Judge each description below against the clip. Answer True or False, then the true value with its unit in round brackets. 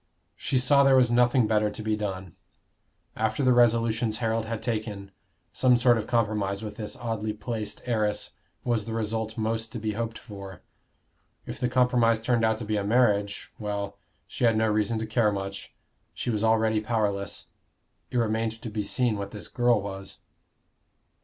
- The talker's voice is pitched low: True (110 Hz)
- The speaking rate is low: False (175 wpm)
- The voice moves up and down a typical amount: False (1.9 semitones)